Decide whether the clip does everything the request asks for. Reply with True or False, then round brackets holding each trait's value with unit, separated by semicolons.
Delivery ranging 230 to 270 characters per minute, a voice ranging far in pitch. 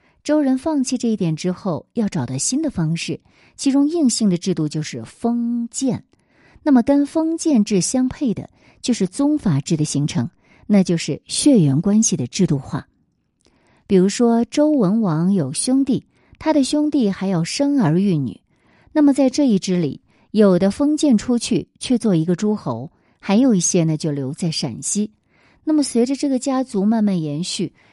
True (245 characters per minute; 7.5 semitones)